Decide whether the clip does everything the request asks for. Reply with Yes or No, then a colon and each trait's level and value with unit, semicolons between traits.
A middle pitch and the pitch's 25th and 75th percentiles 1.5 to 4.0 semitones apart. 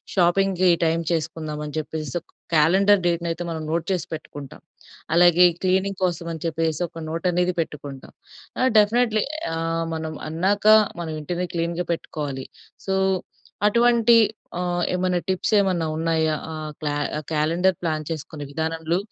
Yes: medium, 165 Hz; narrow, 2.5 semitones